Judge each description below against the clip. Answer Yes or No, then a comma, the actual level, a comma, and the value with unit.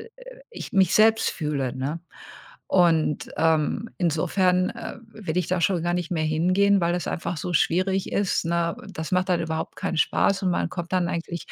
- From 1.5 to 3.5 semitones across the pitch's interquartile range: Yes, narrow, 2.5 semitones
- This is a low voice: No, medium, 175 Hz